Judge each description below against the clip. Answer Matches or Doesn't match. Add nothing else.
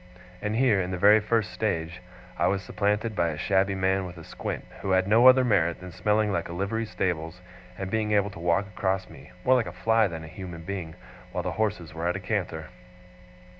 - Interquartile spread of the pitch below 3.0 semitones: Doesn't match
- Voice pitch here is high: Doesn't match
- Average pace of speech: Doesn't match